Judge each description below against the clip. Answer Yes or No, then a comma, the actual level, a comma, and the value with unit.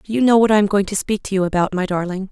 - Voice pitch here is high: Yes, high, 200 Hz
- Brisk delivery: Yes, fast, 365 wpm